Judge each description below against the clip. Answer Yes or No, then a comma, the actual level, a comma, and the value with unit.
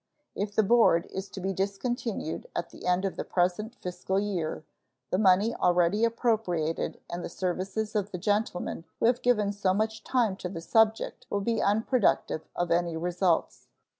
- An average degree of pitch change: Yes, average, 3.6 semitones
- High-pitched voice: Yes, high, 195 Hz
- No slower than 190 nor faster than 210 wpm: No, average, 170 wpm